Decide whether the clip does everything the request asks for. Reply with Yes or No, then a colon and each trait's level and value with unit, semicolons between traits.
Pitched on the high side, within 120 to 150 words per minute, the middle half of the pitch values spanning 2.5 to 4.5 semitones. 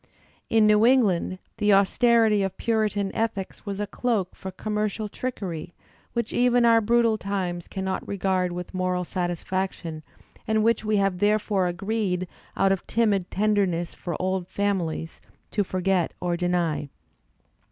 Yes: high, 195 Hz; average, 140 wpm; average, 3.0 semitones